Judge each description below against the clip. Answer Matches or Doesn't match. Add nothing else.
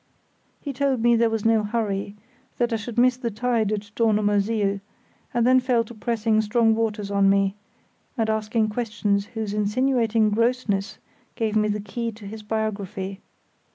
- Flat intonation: Matches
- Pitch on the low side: Doesn't match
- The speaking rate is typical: Matches